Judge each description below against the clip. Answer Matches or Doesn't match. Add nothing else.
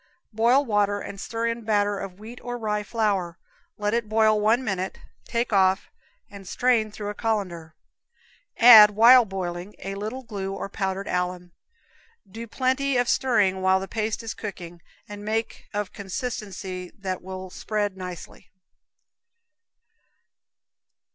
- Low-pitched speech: Doesn't match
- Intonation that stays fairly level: Doesn't match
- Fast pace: Doesn't match